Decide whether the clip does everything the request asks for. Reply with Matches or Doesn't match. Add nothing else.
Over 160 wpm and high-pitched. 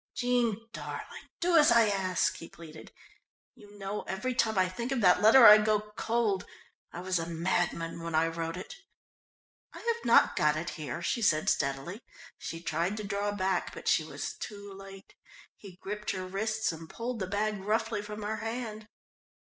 Matches